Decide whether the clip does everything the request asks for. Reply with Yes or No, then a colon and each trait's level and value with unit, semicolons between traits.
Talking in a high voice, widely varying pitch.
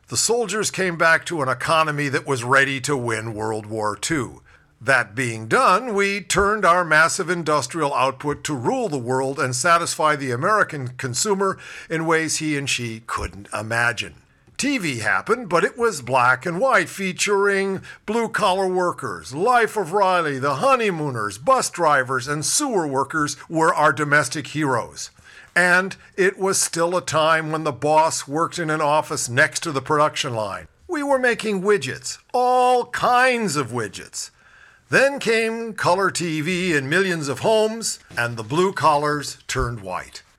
No: medium, 160 Hz; wide, 6.0 semitones